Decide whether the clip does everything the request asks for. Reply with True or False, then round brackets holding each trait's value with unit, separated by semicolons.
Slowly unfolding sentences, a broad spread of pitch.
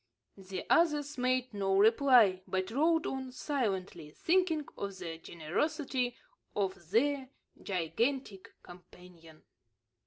True (100 wpm; 7.0 semitones)